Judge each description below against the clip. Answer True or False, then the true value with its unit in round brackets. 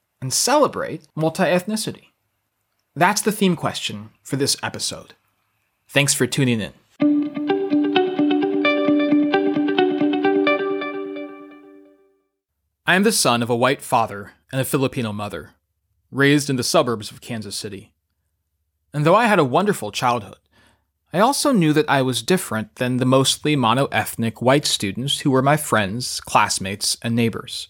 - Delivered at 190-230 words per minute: False (135 wpm)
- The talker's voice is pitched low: True (120 Hz)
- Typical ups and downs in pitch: False (7.0 semitones)